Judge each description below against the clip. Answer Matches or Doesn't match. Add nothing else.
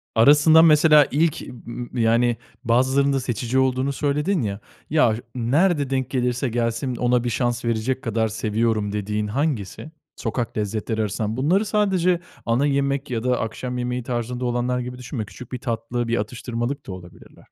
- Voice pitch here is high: Doesn't match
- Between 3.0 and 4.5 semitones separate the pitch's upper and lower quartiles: Matches